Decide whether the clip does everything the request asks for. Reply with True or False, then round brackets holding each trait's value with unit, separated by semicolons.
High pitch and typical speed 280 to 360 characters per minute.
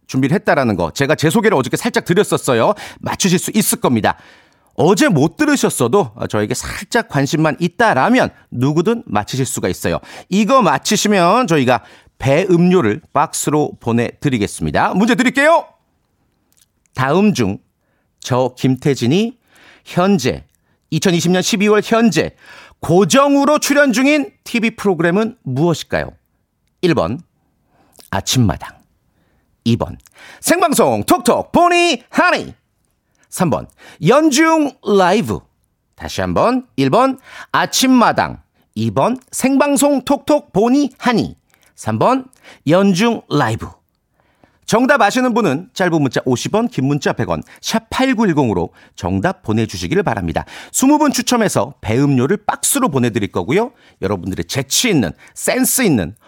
False (200 Hz; 255 characters per minute)